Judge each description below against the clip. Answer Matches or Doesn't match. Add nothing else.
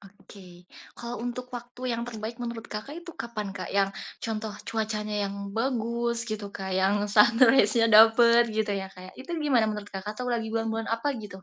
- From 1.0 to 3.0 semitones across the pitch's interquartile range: Matches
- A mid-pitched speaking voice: Doesn't match